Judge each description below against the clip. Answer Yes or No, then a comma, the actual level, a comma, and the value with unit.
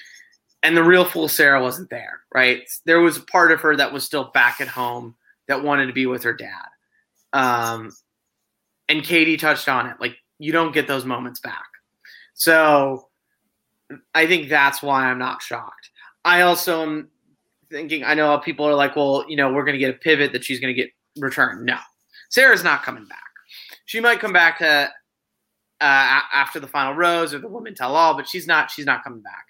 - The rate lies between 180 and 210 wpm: Yes, average, 200 wpm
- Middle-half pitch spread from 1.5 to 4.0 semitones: Yes, average, 3.7 semitones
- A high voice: No, medium, 150 Hz